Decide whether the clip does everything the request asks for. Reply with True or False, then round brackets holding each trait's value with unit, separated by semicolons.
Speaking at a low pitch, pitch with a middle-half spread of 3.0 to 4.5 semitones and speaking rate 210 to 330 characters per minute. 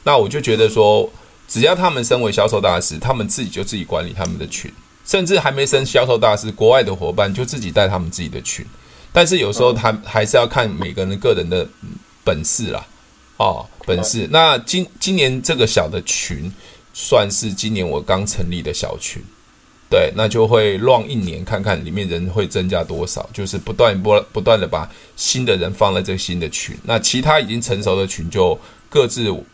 False (105 Hz; 5.3 semitones; 295 characters per minute)